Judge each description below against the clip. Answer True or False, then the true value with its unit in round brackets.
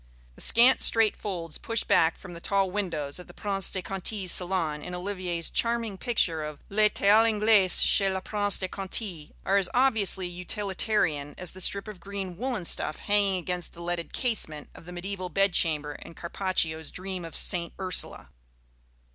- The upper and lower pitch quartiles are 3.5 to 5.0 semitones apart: False (3.1 semitones)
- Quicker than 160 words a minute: True (180 wpm)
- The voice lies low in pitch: False (185 Hz)